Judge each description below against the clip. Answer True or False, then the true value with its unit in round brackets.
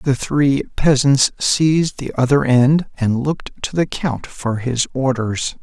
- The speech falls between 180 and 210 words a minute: False (160 wpm)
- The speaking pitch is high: False (135 Hz)